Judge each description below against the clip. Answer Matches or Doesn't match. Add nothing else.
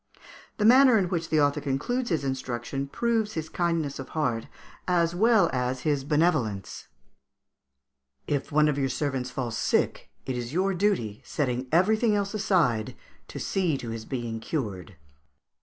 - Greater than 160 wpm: Doesn't match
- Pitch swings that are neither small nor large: Doesn't match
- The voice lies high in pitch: Doesn't match